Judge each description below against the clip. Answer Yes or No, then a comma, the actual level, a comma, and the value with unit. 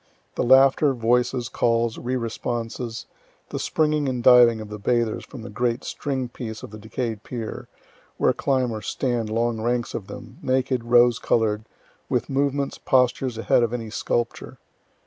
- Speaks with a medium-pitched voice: No, low, 120 Hz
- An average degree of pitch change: No, narrow, 2.0 semitones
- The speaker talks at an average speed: Yes, average, 160 wpm